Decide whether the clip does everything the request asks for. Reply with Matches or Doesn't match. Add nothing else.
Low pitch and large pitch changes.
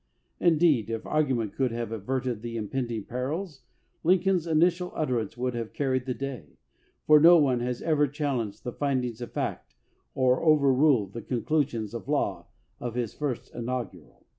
Doesn't match